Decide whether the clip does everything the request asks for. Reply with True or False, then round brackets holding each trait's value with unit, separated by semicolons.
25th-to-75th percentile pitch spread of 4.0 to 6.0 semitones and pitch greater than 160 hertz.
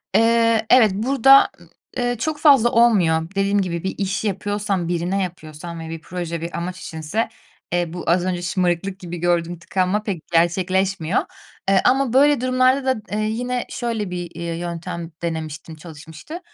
True (4.9 semitones; 185 Hz)